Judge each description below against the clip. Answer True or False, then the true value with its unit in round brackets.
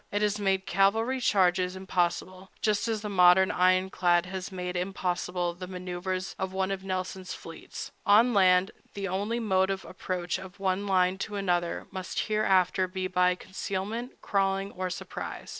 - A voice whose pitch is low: False (190 Hz)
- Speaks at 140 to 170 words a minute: True (160 wpm)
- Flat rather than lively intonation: True (1.3 semitones)